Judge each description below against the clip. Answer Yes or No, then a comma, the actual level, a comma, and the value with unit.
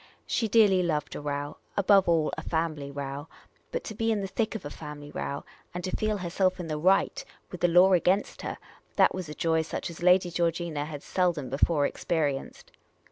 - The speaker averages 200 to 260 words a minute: Yes, fast, 205 wpm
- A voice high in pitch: No, medium, 170 Hz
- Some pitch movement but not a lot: Yes, average, 4.0 semitones